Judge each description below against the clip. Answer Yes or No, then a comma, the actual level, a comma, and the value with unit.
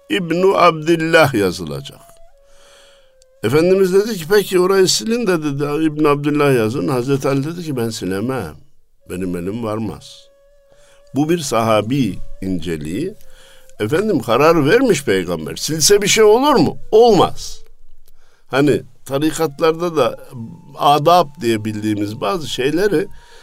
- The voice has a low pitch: No, medium, 150 Hz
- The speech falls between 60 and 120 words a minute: Yes, average, 115 wpm